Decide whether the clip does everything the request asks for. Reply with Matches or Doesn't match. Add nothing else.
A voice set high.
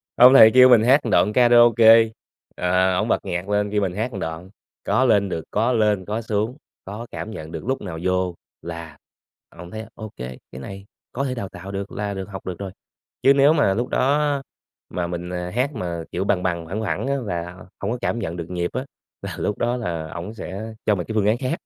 Doesn't match